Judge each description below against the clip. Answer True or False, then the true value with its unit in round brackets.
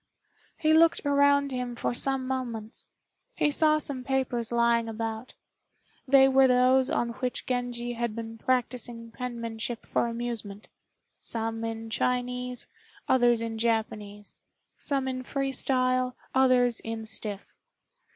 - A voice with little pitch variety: True (2.3 semitones)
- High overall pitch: True (245 Hz)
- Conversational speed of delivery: False (125 wpm)